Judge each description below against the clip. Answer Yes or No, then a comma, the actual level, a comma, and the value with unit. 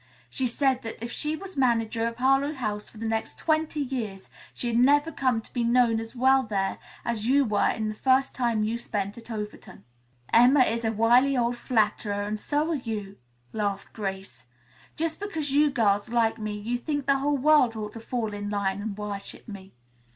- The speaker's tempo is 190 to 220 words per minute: Yes, average, 195 wpm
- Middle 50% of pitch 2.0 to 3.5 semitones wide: No, average, 4.0 semitones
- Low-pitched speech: No, high, 235 Hz